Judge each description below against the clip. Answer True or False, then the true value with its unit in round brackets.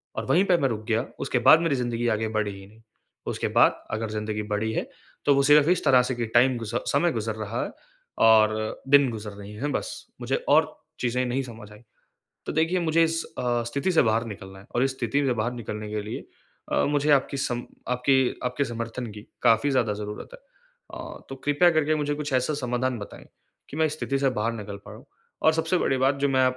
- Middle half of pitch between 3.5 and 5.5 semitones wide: True (4.5 semitones)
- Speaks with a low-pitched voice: True (125 Hz)